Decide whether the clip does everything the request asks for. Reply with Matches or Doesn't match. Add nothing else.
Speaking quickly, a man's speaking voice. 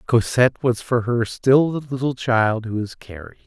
Doesn't match